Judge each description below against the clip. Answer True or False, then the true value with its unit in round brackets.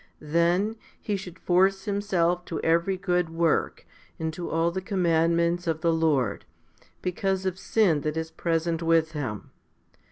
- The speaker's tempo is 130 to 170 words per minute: True (150 wpm)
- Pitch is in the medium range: True (170 Hz)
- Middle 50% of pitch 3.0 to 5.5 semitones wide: False (2.4 semitones)